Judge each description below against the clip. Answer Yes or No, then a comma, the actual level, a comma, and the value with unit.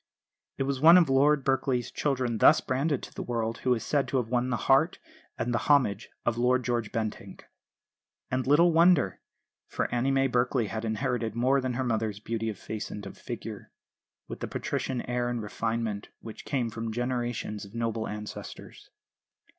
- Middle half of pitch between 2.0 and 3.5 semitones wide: Yes, average, 3.0 semitones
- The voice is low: Yes, low, 120 Hz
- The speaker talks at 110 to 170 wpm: No, average, 180 wpm